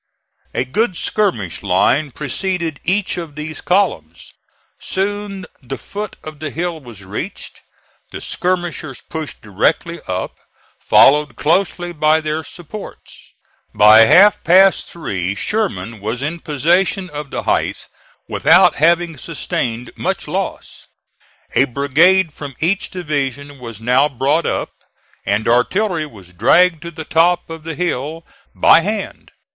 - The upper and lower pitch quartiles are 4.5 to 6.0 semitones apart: Yes, wide, 5.5 semitones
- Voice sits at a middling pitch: Yes, medium, 155 Hz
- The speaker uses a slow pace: Yes, slow, 130 wpm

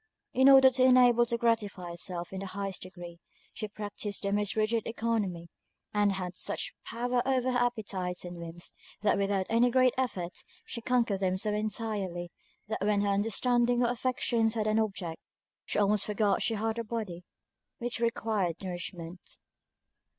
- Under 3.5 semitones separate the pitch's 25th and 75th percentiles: No, average, 3.8 semitones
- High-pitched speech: Yes, high, 210 Hz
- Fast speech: No, average, 165 wpm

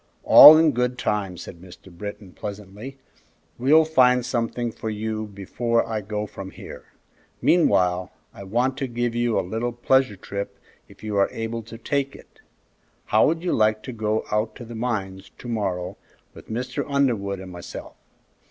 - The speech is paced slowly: No, average, 170 wpm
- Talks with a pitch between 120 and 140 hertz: No, low, 110 Hz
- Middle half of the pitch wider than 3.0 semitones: Yes, average, 3.7 semitones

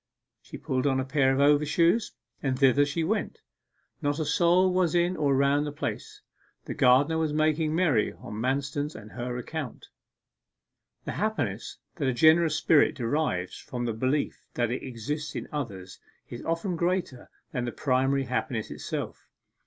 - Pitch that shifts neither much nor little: Yes, average, 3.7 semitones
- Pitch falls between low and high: Yes, medium, 145 Hz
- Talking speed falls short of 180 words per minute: Yes, average, 160 wpm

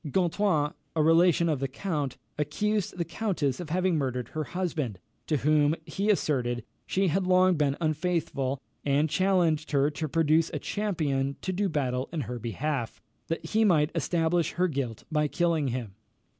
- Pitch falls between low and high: Yes, medium, 155 Hz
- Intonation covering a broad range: No, average, 4.2 semitones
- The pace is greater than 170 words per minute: No, average, 165 wpm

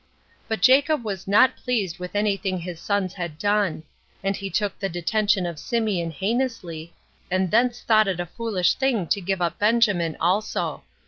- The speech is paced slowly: No, average, 175 wpm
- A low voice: No, high, 195 Hz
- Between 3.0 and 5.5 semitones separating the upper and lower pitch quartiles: Yes, average, 3.7 semitones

